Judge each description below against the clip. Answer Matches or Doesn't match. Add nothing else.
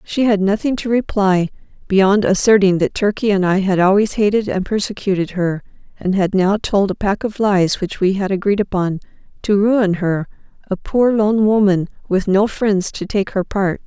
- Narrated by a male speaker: Doesn't match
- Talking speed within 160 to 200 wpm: Matches